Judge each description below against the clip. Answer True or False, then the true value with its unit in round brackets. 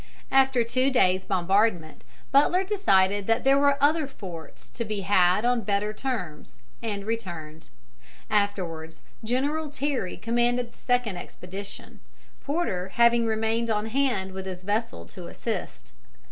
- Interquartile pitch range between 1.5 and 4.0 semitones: False (5.2 semitones)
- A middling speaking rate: False (130 wpm)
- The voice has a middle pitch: False (220 Hz)